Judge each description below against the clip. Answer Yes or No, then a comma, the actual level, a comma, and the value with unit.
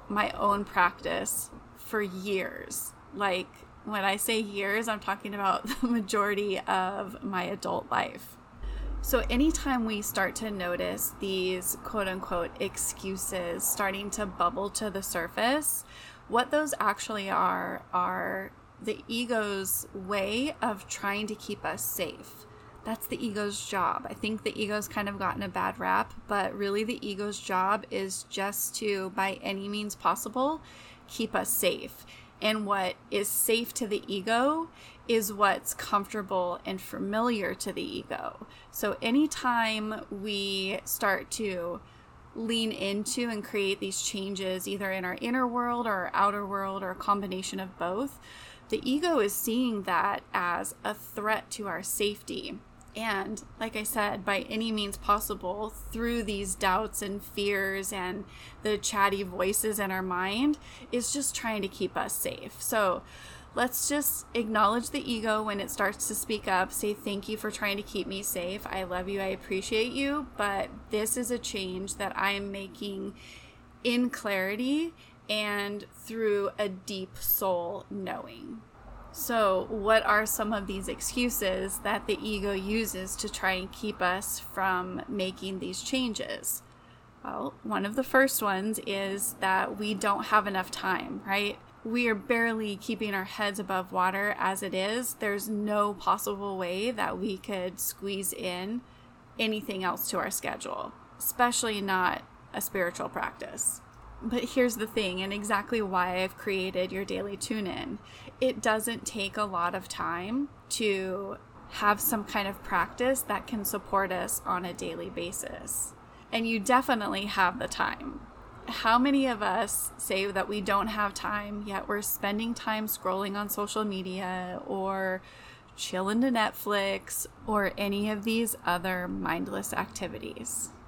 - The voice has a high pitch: Yes, high, 205 Hz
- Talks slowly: No, average, 155 wpm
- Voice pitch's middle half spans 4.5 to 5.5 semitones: No, narrow, 2.5 semitones